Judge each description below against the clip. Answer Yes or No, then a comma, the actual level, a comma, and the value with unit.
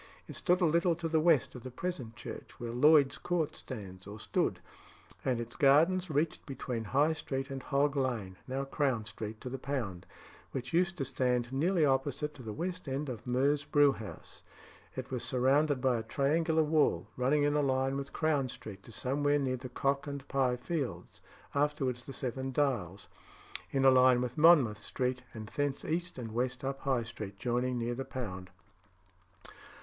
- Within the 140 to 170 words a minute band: No, average, 180 wpm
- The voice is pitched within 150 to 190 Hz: No, low, 135 Hz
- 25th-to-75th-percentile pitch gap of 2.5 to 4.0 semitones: Yes, average, 3.1 semitones